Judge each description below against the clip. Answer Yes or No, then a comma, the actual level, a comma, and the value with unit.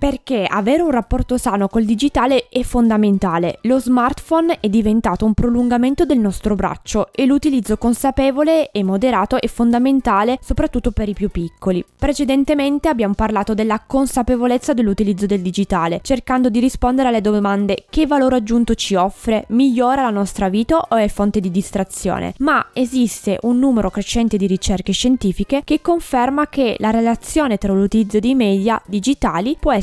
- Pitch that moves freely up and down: No, average, 4.2 semitones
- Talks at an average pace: Yes, average, 155 wpm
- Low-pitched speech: No, high, 235 Hz